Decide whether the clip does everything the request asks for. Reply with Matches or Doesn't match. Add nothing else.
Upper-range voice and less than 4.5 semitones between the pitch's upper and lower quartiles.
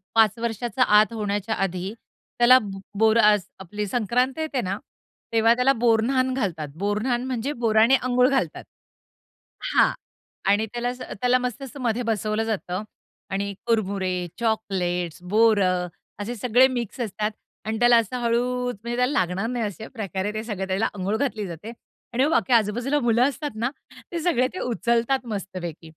Matches